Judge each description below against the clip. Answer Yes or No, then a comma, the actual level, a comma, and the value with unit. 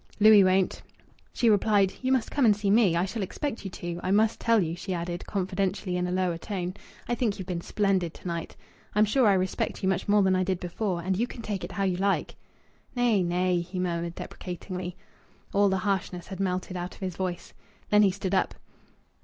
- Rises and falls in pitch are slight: Yes, narrow, 2.3 semitones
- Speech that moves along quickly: Yes, fast, 220 wpm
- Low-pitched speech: No, high, 190 Hz